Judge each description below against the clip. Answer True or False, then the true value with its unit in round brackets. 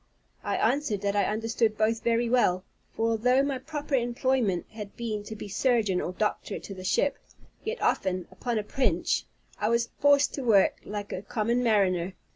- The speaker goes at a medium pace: True (180 wpm)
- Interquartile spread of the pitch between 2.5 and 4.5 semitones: True (3.5 semitones)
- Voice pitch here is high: True (225 Hz)